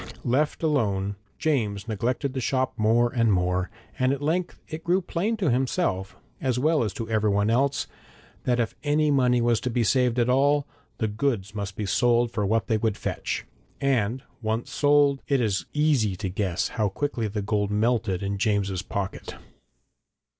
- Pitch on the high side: No, low, 120 Hz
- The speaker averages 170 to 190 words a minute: Yes, average, 175 wpm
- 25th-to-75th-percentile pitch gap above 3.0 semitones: Yes, average, 5.0 semitones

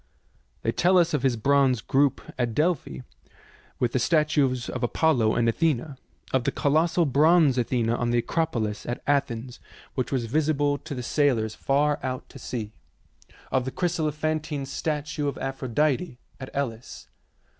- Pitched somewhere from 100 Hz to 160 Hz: Yes, medium, 140 Hz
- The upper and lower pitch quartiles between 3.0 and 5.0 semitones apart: Yes, average, 3.9 semitones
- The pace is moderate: Yes, average, 150 wpm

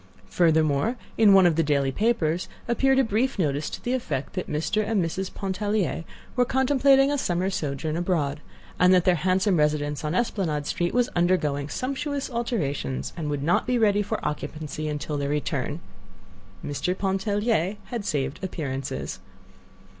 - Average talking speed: Yes, average, 155 wpm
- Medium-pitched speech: Yes, medium, 180 Hz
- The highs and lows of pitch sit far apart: Yes, wide, 6.4 semitones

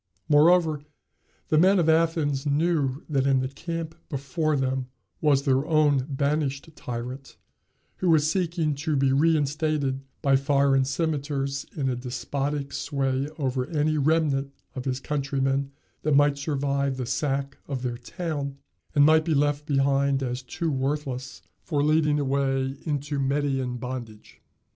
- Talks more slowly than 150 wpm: Yes, average, 140 wpm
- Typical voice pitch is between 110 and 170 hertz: Yes, medium, 140 Hz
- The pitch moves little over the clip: Yes, narrow, 2.2 semitones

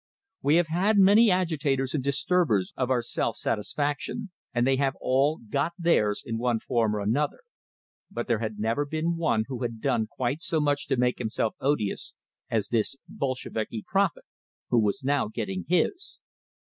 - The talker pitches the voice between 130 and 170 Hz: Yes, low, 135 Hz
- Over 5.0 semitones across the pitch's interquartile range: Yes, wide, 5.6 semitones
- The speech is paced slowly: No, average, 170 wpm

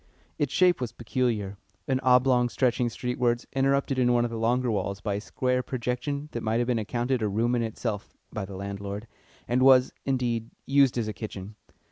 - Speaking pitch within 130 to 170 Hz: No, low, 120 Hz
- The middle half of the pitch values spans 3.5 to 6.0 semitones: No, average, 2.8 semitones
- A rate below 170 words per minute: No, average, 190 wpm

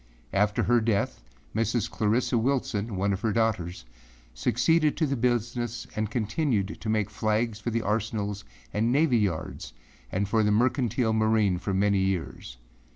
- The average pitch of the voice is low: Yes, low, 110 Hz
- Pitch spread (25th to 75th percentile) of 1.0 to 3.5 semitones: Yes, average, 2.8 semitones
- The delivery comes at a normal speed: Yes, average, 155 wpm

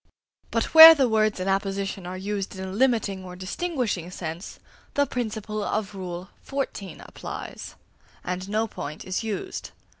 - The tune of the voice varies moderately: Yes, average, 3.2 semitones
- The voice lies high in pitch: Yes, high, 200 Hz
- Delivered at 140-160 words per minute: Yes, average, 150 wpm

